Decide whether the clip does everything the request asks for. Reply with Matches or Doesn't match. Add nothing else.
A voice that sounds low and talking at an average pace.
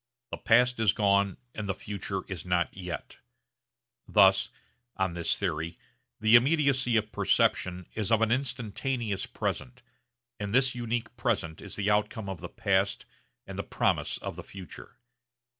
Matches